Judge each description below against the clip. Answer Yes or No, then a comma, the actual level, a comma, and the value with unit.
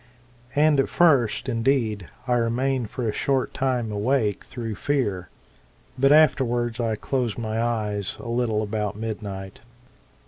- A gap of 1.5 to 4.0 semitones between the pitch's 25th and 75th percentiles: Yes, average, 3.6 semitones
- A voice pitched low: Yes, low, 115 Hz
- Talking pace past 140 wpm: No, slow, 135 wpm